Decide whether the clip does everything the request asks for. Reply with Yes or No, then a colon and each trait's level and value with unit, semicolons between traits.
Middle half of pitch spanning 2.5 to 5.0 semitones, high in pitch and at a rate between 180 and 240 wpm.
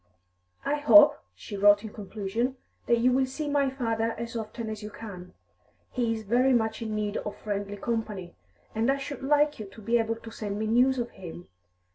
Yes: average, 3.4 semitones; high, 225 Hz; average, 200 wpm